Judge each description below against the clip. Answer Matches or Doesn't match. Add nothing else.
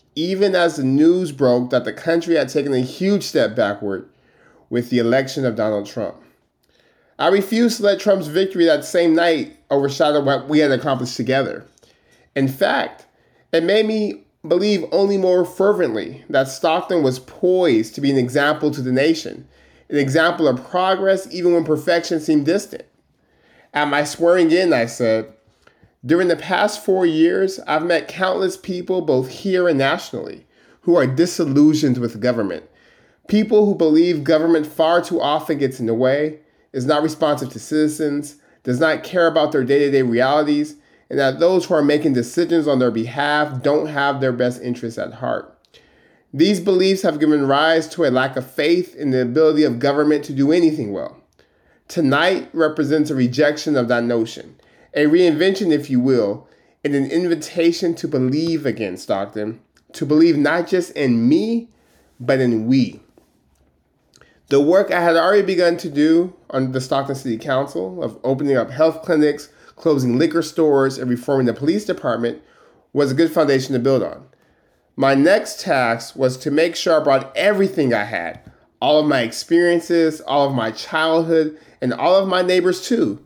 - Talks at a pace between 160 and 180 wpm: Matches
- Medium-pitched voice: Matches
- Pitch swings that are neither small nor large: Matches